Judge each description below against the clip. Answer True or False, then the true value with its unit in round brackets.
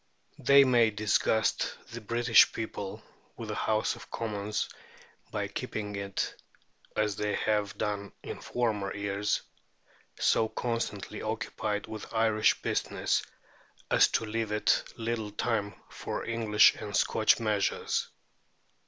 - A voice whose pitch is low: True (110 Hz)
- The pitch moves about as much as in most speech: False (1.6 semitones)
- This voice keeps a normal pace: False (120 wpm)